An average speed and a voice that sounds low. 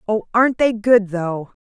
No: average, 185 wpm; high, 210 Hz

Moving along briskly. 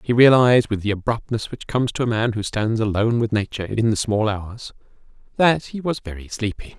Yes: fast, 210 wpm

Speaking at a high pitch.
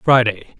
No: low, 120 Hz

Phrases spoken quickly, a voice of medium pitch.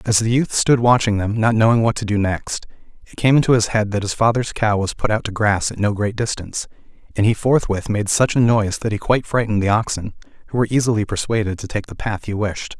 No: fast, 250 wpm; low, 110 Hz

